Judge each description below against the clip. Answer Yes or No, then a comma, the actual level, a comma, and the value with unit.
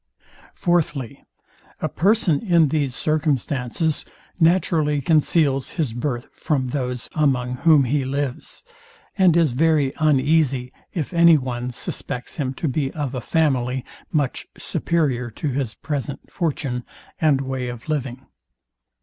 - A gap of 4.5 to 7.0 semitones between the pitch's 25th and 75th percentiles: No, average, 3.8 semitones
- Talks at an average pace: No, slow, 125 wpm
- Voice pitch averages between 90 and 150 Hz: Yes, medium, 140 Hz